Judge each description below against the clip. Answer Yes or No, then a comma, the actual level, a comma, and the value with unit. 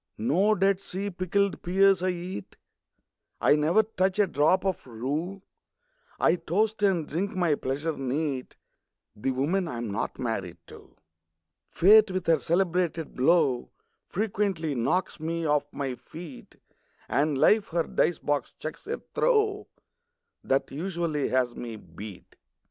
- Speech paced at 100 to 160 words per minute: Yes, slow, 135 wpm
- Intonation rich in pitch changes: Yes, wide, 5.7 semitones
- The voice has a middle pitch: Yes, medium, 165 Hz